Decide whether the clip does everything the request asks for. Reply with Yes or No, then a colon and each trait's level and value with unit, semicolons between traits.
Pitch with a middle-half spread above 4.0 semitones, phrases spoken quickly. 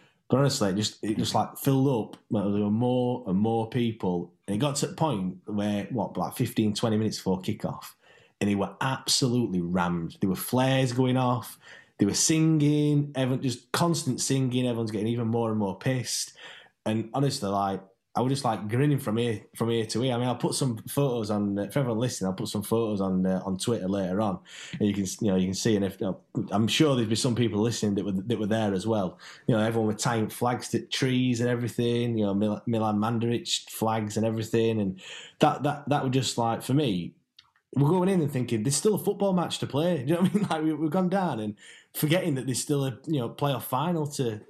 Yes: average, 4.7 semitones; fast, 230 wpm